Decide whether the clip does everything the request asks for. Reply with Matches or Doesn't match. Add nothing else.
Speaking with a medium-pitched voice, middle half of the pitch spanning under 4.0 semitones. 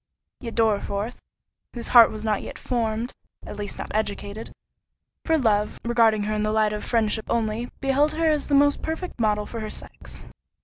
Doesn't match